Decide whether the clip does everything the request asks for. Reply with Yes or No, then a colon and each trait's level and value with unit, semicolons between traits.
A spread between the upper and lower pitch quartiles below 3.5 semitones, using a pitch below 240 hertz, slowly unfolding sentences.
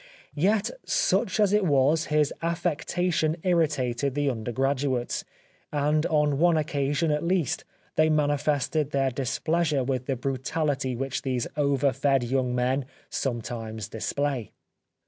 Yes: average, 3.1 semitones; medium, 140 Hz; slow, 130 wpm